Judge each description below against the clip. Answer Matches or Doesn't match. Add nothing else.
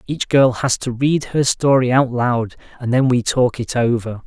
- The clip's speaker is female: Doesn't match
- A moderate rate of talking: Doesn't match